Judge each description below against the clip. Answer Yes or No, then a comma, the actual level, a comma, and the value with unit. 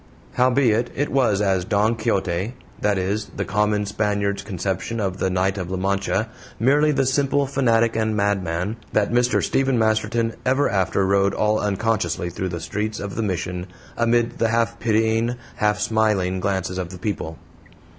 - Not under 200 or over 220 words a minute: No, average, 165 wpm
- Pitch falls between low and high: No, low, 105 Hz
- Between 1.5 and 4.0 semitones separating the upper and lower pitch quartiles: Yes, average, 3.2 semitones